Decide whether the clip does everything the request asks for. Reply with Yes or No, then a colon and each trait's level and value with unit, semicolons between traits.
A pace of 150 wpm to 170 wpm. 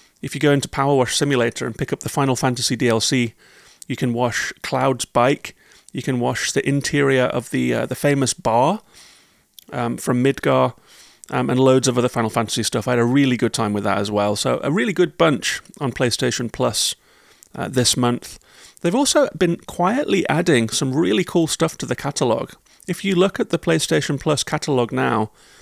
No: average, 195 wpm